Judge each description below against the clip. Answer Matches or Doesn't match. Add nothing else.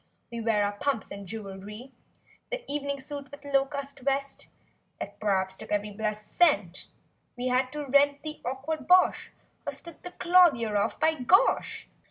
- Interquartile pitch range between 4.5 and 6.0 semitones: Matches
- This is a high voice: Matches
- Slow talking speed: Doesn't match